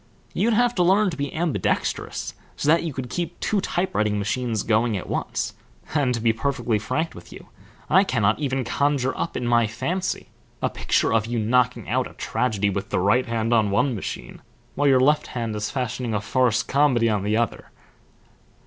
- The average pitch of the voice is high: No, low, 125 Hz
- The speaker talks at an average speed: Yes, average, 195 wpm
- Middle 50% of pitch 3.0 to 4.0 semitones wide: No, average, 5.0 semitones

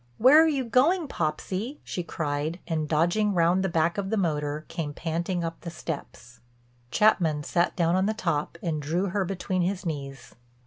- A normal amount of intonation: Yes, average, 4.0 semitones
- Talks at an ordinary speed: Yes, average, 180 wpm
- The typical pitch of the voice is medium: Yes, medium, 170 Hz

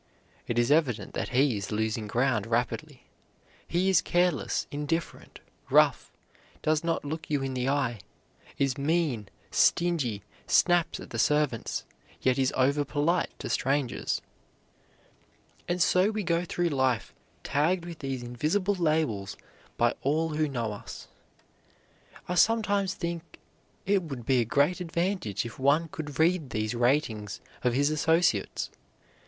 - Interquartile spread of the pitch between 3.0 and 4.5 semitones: No, wide, 5.6 semitones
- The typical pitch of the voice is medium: Yes, medium, 145 Hz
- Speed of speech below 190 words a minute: Yes, average, 140 wpm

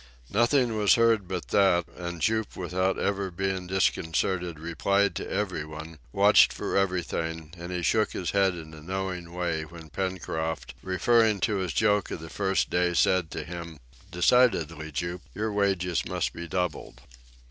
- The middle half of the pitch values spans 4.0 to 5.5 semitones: No, average, 2.8 semitones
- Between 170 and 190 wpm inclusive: No, average, 160 wpm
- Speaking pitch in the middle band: No, very low, 90 Hz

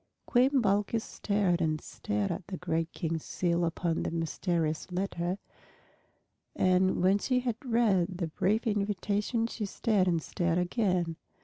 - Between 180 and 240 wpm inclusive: No, average, 140 wpm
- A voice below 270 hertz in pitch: Yes, medium, 185 Hz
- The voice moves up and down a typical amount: Yes, average, 3.6 semitones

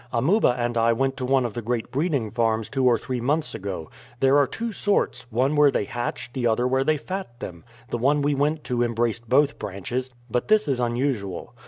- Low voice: Yes, low, 125 Hz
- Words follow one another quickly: Yes, fast, 215 wpm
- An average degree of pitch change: Yes, average, 3.3 semitones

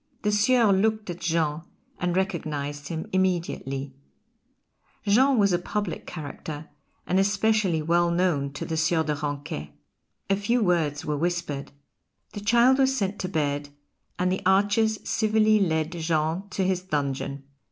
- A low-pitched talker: No, medium, 175 Hz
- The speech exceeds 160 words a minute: No, average, 145 wpm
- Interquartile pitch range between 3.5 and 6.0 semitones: Yes, average, 4.9 semitones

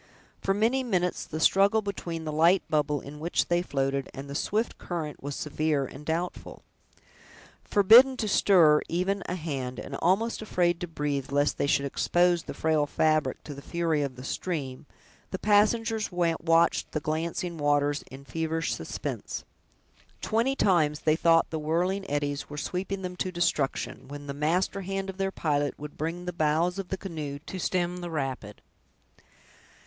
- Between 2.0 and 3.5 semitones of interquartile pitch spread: No, average, 4.1 semitones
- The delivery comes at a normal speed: Yes, average, 170 wpm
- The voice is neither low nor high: Yes, medium, 165 Hz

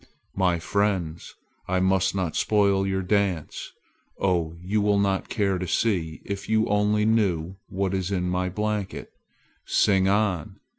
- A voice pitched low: Yes, very low, 95 Hz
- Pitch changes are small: Yes, narrow, 2.1 semitones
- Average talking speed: Yes, average, 145 wpm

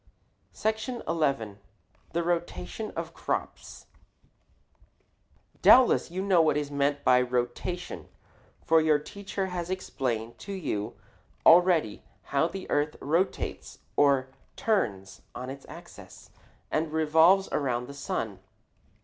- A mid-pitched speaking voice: Yes, medium, 155 Hz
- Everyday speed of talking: No, slow, 115 wpm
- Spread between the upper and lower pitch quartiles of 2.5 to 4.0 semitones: No, wide, 5.5 semitones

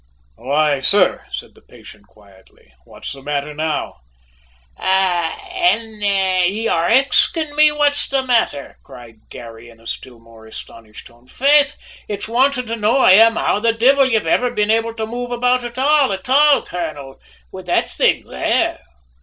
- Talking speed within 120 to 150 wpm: No, average, 160 wpm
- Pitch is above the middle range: Yes, high, 205 Hz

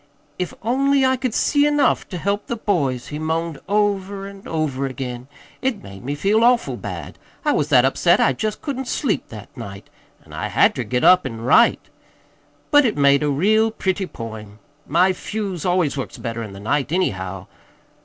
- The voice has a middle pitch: Yes, medium, 175 Hz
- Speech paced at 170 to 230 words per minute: Yes, average, 185 wpm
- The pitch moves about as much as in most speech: No, wide, 8.7 semitones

